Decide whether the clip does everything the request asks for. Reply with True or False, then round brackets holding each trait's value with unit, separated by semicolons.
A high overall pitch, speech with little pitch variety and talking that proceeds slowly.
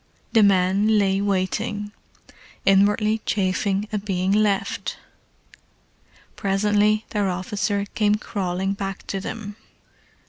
True (200 Hz; 1.5 semitones; 100 wpm)